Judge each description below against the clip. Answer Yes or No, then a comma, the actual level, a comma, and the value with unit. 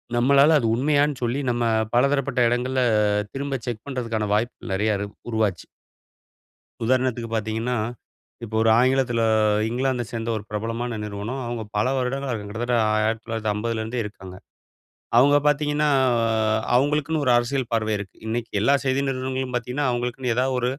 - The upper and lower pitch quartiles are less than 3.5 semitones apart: Yes, average, 2.9 semitones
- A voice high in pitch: No, low, 120 Hz